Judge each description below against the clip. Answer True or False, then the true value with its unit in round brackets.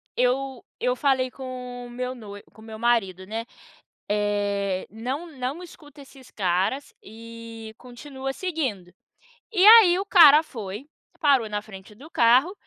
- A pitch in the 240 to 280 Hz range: True (245 Hz)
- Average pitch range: True (4.4 semitones)